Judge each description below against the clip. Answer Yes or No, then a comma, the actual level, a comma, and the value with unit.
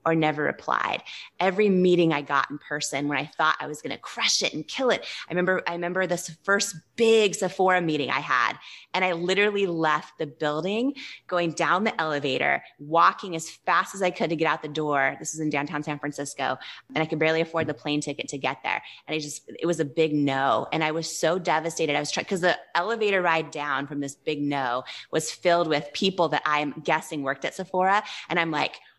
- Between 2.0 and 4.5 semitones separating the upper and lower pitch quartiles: Yes, average, 3.4 semitones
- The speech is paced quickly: Yes, fast, 225 wpm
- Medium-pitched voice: Yes, medium, 160 Hz